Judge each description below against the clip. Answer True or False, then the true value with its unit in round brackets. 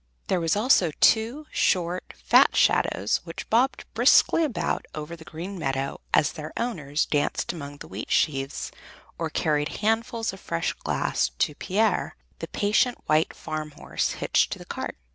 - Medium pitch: True (170 Hz)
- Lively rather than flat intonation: True (6.8 semitones)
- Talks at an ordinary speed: True (160 wpm)